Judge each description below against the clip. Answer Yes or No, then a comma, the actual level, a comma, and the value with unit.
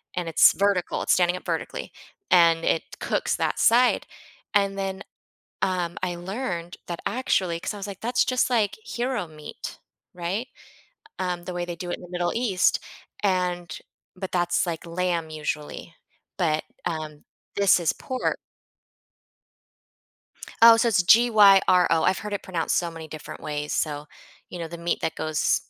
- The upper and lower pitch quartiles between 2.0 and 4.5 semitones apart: Yes, average, 3.0 semitones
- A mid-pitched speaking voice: Yes, medium, 180 Hz